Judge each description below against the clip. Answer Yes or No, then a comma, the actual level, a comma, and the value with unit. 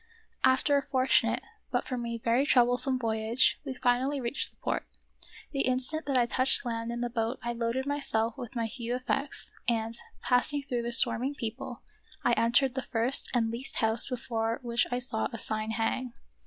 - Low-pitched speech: No, high, 245 Hz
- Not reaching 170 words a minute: No, average, 185 wpm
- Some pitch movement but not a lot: No, narrow, 2.1 semitones